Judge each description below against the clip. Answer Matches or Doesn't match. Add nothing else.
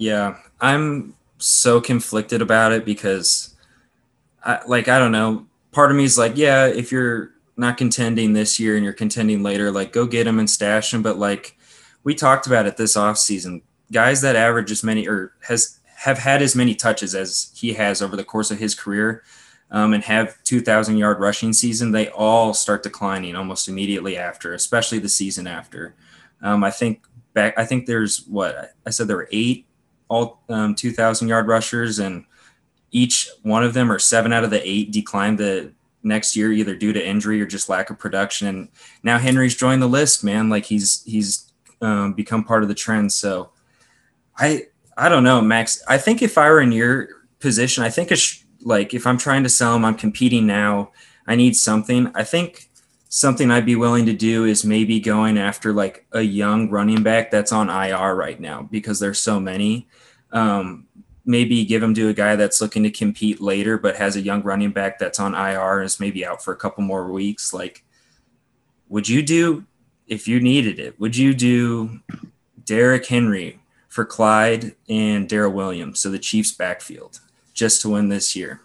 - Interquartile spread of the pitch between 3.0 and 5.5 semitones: Doesn't match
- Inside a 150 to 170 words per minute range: Doesn't match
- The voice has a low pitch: Matches